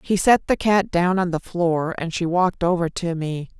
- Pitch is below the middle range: No, medium, 175 Hz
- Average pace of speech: No, fast, 235 wpm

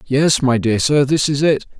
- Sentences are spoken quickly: Yes, fast, 235 wpm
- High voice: No, low, 135 Hz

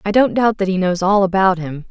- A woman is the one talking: Yes, female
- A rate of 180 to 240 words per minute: No, fast, 285 wpm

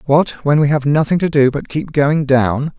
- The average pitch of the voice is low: No, medium, 145 Hz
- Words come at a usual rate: No, fast, 235 wpm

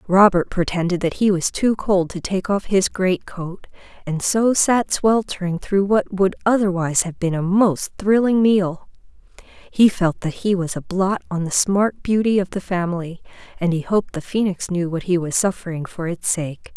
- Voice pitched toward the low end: No, medium, 185 Hz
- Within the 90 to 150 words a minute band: No, average, 195 wpm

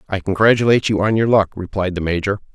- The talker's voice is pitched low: Yes, low, 100 Hz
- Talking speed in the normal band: No, fast, 210 wpm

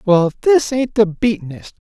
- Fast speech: No, average, 190 wpm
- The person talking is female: No, male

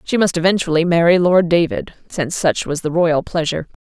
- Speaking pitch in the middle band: Yes, medium, 170 Hz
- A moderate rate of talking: Yes, average, 190 wpm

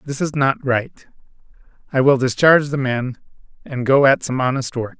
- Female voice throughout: No, male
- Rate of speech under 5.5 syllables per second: Yes, 5.0 syllables/s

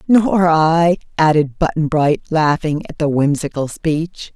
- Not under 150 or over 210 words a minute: No, average, 140 wpm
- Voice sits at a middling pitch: Yes, medium, 160 Hz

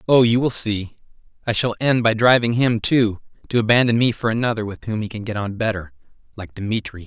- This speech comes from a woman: No, male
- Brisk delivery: Yes, fast, 210 wpm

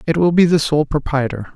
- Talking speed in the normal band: No, fast, 230 wpm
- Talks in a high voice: No, medium, 150 Hz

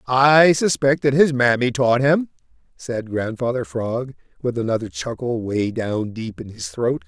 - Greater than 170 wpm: No, average, 160 wpm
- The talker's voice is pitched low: Yes, low, 125 Hz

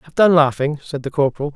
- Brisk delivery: Yes, fast, 230 wpm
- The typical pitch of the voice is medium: Yes, medium, 145 Hz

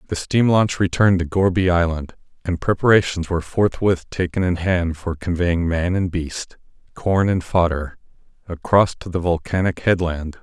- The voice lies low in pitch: Yes, very low, 90 Hz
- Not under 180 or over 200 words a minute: No, average, 155 wpm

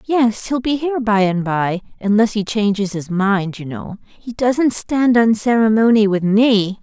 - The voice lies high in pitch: Yes, high, 215 Hz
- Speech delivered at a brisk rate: No, average, 185 wpm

